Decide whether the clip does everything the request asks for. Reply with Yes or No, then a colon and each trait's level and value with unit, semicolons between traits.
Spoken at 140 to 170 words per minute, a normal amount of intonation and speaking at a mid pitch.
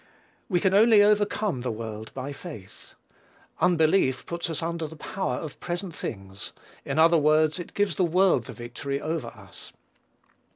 No: average, 160 wpm; wide, 5.9 semitones; medium, 160 Hz